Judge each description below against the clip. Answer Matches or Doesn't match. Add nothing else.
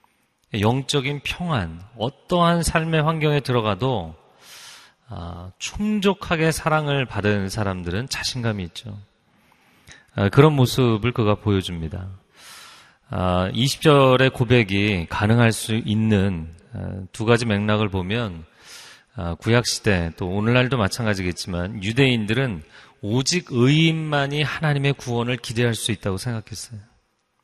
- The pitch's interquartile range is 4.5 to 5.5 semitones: Matches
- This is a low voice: Matches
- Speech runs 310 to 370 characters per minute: Doesn't match